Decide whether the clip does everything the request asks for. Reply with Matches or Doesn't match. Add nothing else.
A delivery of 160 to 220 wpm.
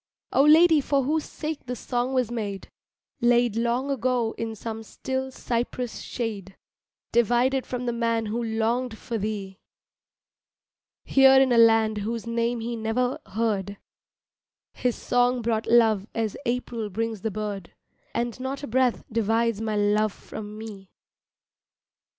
Doesn't match